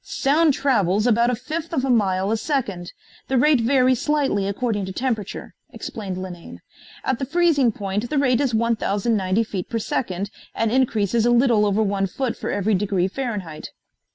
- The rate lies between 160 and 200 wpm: Yes, average, 175 wpm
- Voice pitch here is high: Yes, high, 225 Hz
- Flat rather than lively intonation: No, average, 4.8 semitones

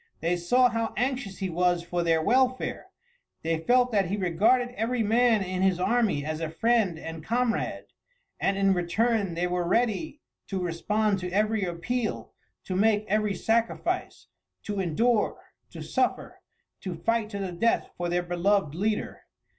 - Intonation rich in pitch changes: No, average, 4.6 semitones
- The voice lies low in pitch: No, high, 200 Hz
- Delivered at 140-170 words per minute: Yes, average, 160 wpm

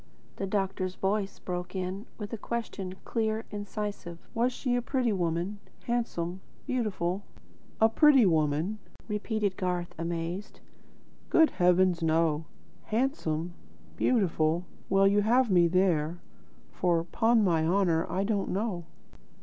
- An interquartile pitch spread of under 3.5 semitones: No, average, 3.9 semitones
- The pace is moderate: No, slow, 125 wpm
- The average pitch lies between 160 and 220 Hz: Yes, high, 190 Hz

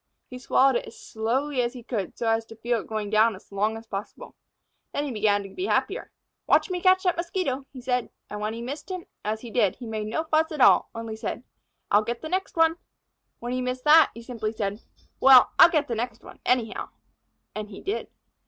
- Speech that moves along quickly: Yes, fast, 225 wpm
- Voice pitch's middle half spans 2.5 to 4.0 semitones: No, average, 4.8 semitones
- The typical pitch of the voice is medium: No, high, 240 Hz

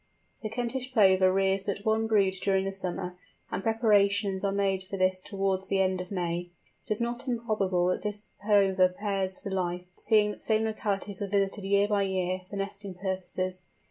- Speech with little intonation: Yes, narrow, 1.9 semitones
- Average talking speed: Yes, average, 190 wpm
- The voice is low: No, high, 195 Hz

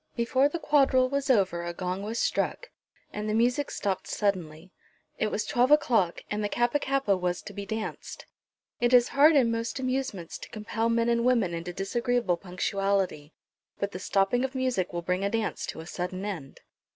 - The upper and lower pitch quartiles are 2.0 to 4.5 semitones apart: No, average, 5.1 semitones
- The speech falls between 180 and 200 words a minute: Yes, average, 190 wpm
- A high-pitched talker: Yes, high, 215 Hz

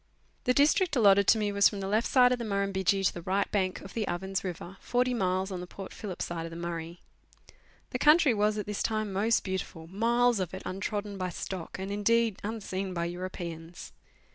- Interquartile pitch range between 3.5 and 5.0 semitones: No, average, 2.8 semitones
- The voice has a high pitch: Yes, high, 195 Hz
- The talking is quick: Yes, fast, 215 wpm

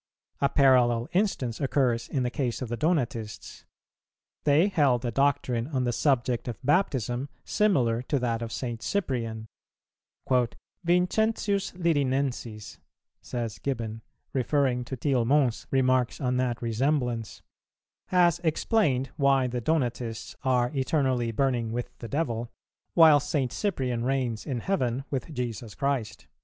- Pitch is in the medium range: No, low, 130 Hz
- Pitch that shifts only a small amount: No, average, 3.3 semitones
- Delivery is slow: Yes, slow, 125 wpm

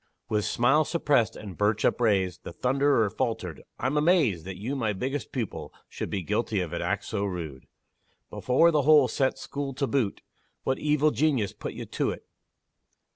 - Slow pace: No, average, 170 wpm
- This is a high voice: No, low, 120 Hz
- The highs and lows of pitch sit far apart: Yes, wide, 5.9 semitones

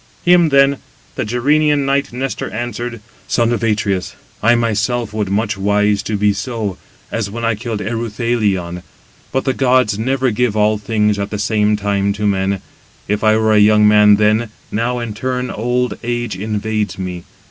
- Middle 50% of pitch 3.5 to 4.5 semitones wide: No, average, 2.7 semitones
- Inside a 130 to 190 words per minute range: Yes, average, 170 wpm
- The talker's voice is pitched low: Yes, low, 110 Hz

